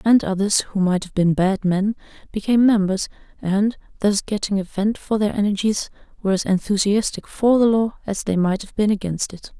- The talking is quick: No, average, 195 wpm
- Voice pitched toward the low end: No, high, 200 Hz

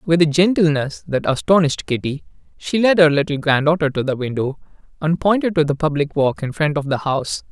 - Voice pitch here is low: No, medium, 155 Hz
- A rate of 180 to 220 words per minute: Yes, average, 200 wpm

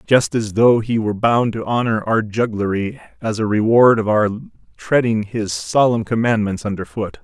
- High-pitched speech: No, low, 110 Hz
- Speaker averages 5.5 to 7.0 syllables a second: No, 4.9 syllables/s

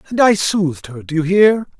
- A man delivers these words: Yes, male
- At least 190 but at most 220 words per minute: No, fast, 235 wpm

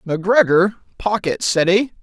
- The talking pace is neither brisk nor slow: No, slow, 90 wpm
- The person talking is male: Yes, male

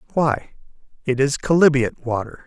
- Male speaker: Yes, male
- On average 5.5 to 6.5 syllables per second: Yes, 5.8 syllables/s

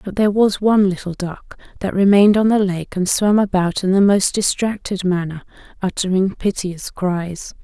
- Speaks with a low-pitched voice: No, high, 190 Hz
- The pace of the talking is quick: No, average, 175 wpm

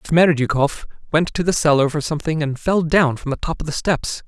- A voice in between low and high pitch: Yes, medium, 155 Hz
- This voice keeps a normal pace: No, fast, 225 wpm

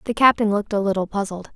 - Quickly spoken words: Yes, fast, 230 wpm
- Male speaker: No, female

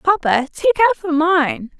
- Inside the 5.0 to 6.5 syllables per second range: Yes, 5.4 syllables/s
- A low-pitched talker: No, very high, 335 Hz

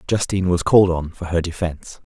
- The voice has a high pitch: No, very low, 90 Hz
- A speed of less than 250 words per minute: Yes, average, 200 wpm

